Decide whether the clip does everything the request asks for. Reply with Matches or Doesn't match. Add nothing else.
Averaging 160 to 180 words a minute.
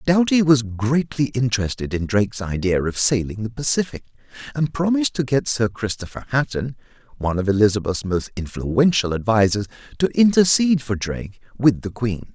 Doesn't match